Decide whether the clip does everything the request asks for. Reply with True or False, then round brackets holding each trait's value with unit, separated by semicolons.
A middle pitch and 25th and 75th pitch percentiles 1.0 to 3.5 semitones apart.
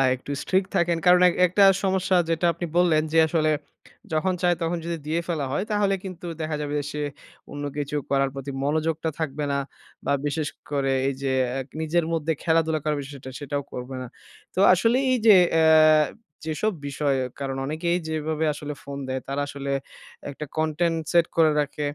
True (155 Hz; 3.2 semitones)